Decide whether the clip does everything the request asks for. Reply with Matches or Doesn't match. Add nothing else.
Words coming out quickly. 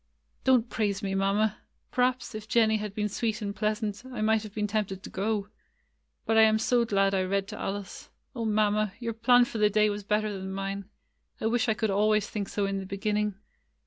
Matches